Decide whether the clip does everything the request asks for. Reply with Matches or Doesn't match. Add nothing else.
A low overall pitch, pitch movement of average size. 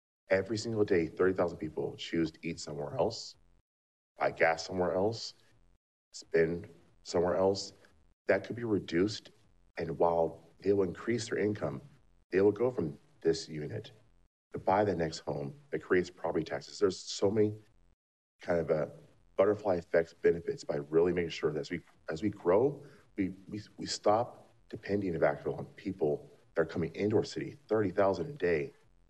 Matches